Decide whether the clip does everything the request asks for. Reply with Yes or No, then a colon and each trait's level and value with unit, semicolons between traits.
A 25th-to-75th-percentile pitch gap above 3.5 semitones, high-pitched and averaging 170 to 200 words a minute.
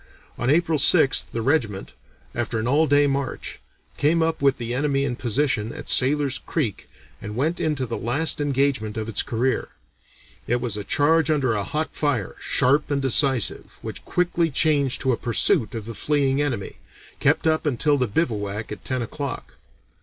No: average, 4.1 semitones; low, 135 Hz; average, 175 wpm